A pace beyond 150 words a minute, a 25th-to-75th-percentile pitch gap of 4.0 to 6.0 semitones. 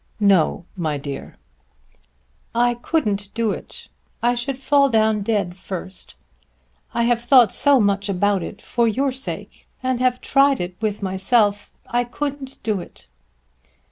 No: average, 140 wpm; average, 4.3 semitones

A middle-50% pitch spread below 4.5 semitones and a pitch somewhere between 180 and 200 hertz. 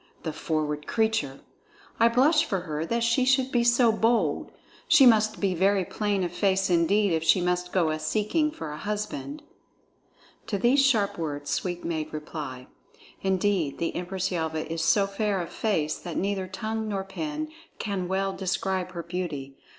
No: average, 4.8 semitones; high, 190 Hz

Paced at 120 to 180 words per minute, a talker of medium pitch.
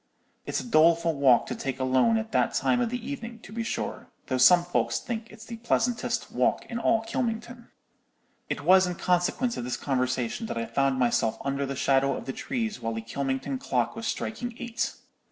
No: average, 200 wpm; medium, 180 Hz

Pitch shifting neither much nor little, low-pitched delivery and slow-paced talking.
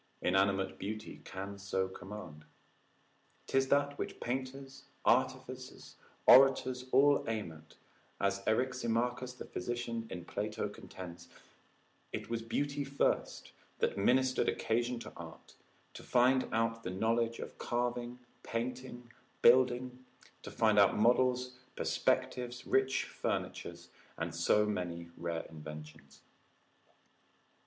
Yes: average, 4.4 semitones; low, 120 Hz; slow, 110 wpm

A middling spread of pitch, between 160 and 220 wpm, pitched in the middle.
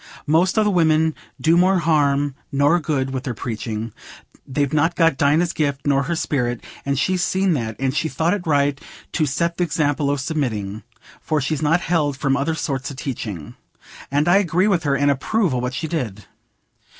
Yes: average, 3.5 semitones; average, 185 wpm; medium, 145 Hz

